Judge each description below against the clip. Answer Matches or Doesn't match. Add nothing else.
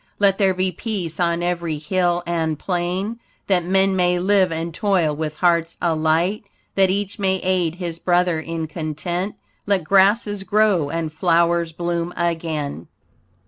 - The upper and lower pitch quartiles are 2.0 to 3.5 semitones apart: Matches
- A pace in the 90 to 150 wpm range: Matches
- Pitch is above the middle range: Doesn't match